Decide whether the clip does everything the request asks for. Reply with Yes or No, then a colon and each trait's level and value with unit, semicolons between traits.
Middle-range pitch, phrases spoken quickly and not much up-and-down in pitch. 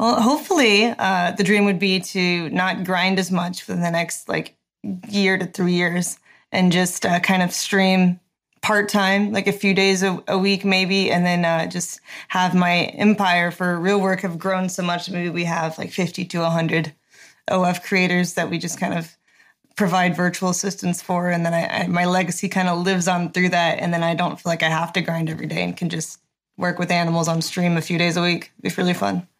Yes: medium, 180 Hz; fast, 220 wpm; narrow, 1.8 semitones